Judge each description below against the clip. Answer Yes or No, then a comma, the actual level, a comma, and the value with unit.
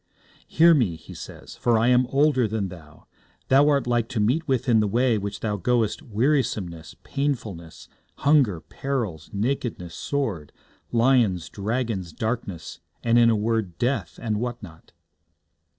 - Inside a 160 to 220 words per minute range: No, average, 150 wpm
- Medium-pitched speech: No, low, 115 Hz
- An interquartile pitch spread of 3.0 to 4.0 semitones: No, average, 4.6 semitones